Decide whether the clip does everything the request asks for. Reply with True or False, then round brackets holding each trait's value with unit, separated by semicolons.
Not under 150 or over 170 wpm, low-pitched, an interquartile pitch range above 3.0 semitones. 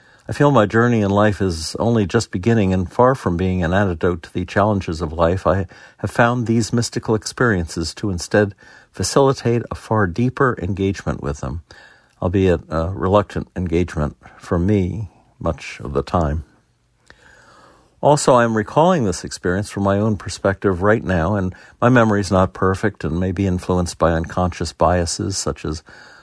True (165 wpm; 95 Hz; 3.8 semitones)